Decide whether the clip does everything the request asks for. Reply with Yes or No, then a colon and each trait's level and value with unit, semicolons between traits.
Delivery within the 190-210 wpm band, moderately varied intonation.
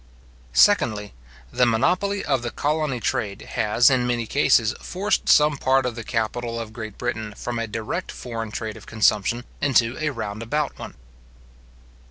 No: average, 160 wpm; average, 3.2 semitones